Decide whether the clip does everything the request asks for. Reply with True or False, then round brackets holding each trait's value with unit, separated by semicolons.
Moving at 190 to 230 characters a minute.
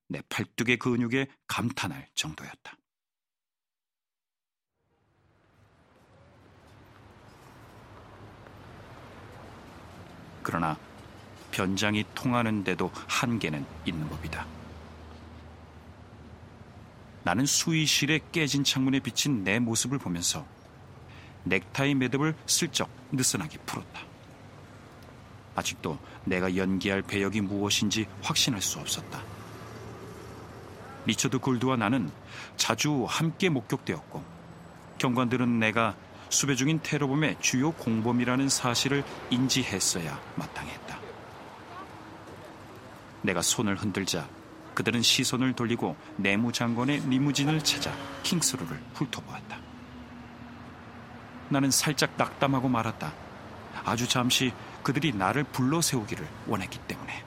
True (220 characters per minute)